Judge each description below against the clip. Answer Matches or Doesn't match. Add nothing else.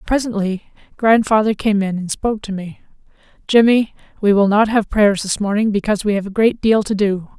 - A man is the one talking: Doesn't match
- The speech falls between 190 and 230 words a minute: Matches